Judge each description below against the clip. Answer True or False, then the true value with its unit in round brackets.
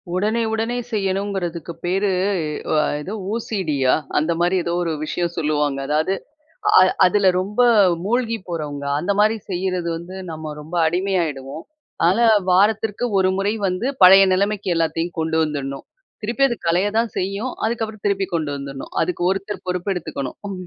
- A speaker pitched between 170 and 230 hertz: True (185 Hz)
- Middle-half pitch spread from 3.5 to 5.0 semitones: True (4.2 semitones)